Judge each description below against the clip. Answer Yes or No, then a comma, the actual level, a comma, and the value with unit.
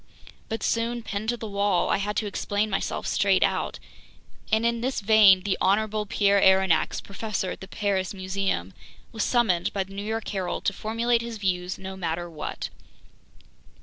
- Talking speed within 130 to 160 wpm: No, average, 175 wpm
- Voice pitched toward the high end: Yes, high, 200 Hz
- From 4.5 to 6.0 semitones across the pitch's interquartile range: No, narrow, 2.6 semitones